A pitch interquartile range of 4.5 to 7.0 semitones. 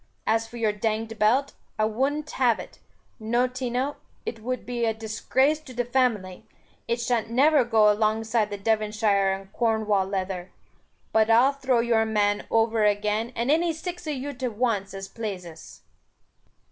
No: average, 3.0 semitones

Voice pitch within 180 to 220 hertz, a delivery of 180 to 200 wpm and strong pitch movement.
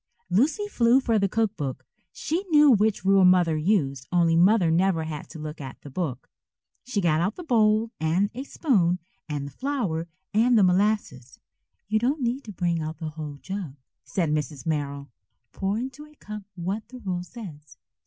Yes: medium, 185 Hz; average, 185 wpm; wide, 6.2 semitones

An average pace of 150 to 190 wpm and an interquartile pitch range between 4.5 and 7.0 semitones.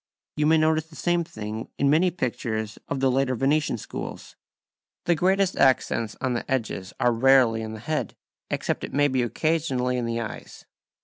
Yes: average, 180 wpm; average, 5.2 semitones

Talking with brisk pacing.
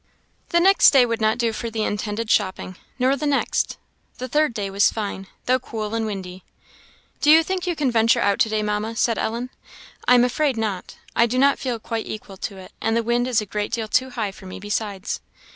Yes: fast, 225 wpm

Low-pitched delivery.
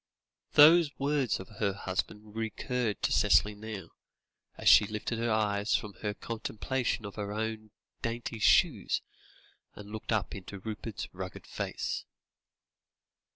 Yes: low, 110 Hz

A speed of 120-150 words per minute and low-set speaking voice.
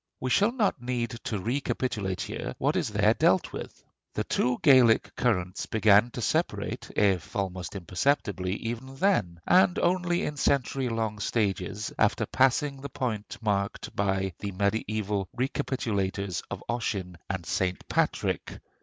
Yes: average, 140 wpm; low, 110 Hz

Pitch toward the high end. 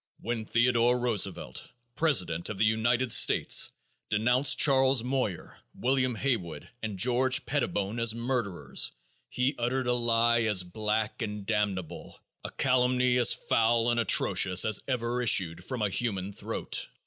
No: low, 115 Hz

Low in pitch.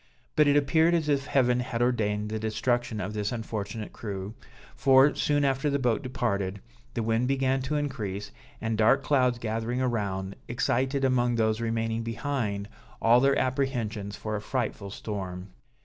Yes: low, 115 Hz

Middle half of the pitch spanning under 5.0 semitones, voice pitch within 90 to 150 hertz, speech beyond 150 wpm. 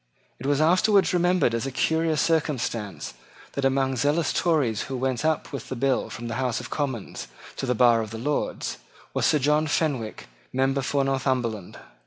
Yes: average, 3.8 semitones; low, 135 Hz; average, 180 wpm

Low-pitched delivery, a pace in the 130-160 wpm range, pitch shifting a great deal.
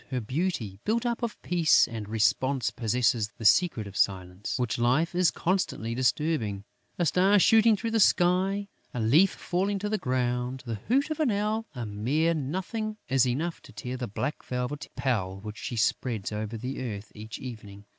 No: low, 130 Hz; average, 180 wpm; wide, 8.8 semitones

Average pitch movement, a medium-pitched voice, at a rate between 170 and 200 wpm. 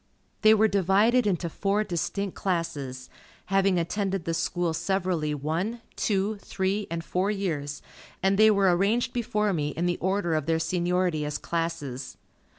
No: average, 3.3 semitones; medium, 180 Hz; average, 155 wpm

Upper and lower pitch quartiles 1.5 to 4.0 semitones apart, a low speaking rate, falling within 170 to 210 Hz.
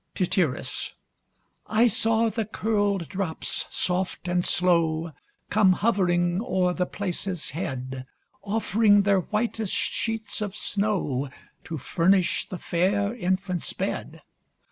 Yes: average, 3.3 semitones; slow, 110 wpm; high, 190 Hz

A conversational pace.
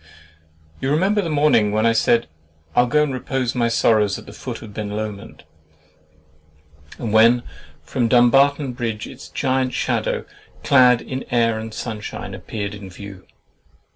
Yes: average, 150 wpm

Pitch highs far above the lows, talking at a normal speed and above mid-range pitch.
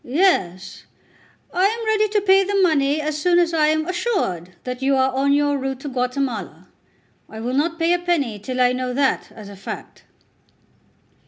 Yes: wide, 5.7 semitones; average, 185 wpm; very high, 280 Hz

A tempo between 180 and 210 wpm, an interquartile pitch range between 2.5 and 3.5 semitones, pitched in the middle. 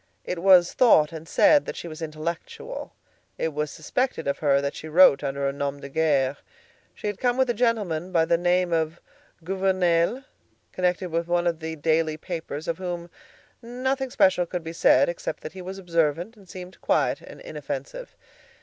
Yes: average, 185 wpm; average, 3.2 semitones; medium, 170 Hz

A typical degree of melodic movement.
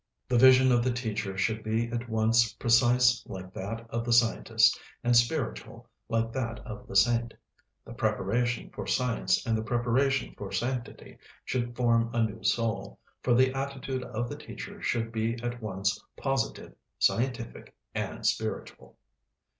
No: narrow, 1.8 semitones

